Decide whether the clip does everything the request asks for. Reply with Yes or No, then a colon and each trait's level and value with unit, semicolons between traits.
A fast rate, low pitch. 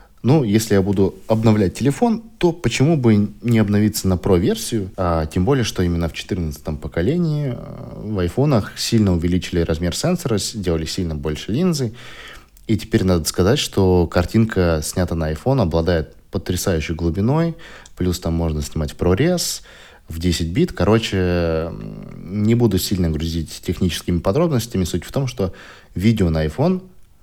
No: average, 145 wpm; very low, 95 Hz